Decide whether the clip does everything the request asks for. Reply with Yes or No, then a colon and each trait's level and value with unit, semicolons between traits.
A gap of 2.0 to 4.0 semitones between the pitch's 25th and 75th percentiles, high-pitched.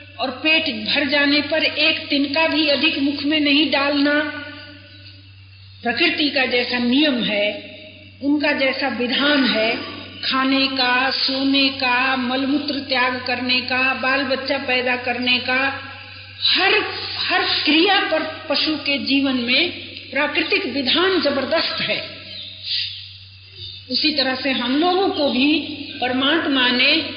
Yes: average, 3.1 semitones; very high, 275 Hz